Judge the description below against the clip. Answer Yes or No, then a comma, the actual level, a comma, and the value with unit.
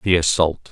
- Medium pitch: No, very low, 85 Hz